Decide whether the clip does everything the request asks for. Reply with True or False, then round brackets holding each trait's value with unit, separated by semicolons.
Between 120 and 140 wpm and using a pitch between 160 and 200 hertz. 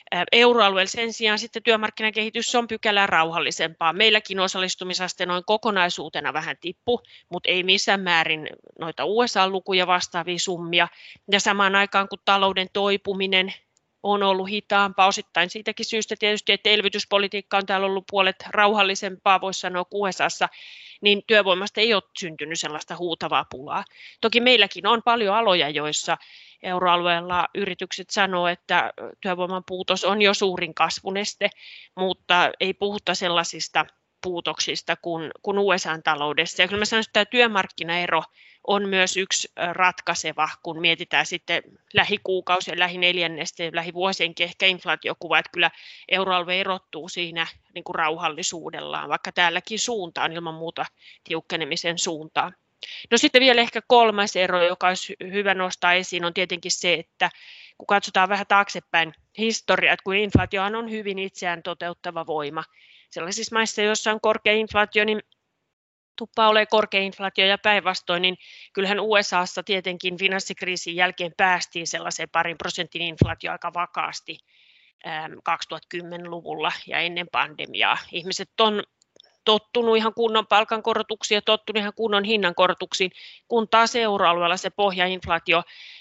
True (130 wpm; 190 Hz)